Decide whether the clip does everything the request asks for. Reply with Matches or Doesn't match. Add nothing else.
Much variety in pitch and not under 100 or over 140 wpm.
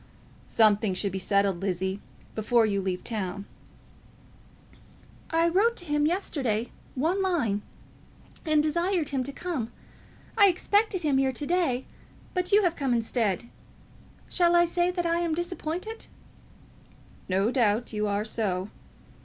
Matches